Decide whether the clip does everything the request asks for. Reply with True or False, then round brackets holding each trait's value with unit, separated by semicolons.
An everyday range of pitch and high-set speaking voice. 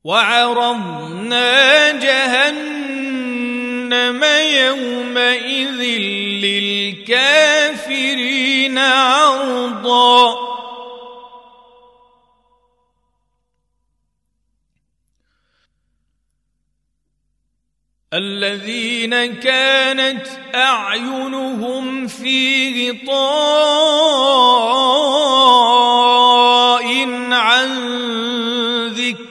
False (1.8 semitones; 245 Hz)